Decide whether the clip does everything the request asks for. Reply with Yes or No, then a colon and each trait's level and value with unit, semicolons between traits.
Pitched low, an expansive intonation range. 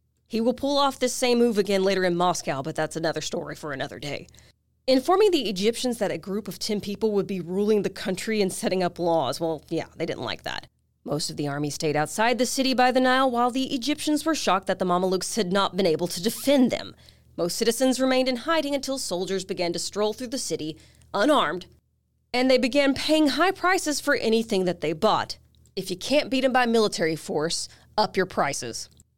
No: high, 210 Hz; wide, 6.5 semitones